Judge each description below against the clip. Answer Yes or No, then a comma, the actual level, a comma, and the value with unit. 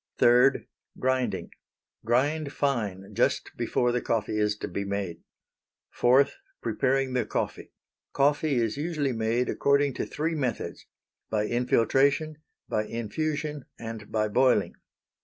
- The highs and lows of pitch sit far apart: No, average, 4.3 semitones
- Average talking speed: No, slow, 120 wpm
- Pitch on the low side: Yes, low, 125 Hz